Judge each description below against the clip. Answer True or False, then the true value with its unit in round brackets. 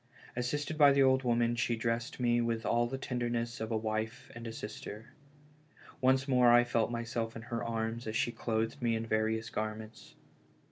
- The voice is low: True (115 Hz)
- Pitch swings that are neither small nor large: False (1.4 semitones)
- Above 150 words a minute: True (185 wpm)